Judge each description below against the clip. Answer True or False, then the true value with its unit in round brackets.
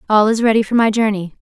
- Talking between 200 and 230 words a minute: False (250 wpm)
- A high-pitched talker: True (215 Hz)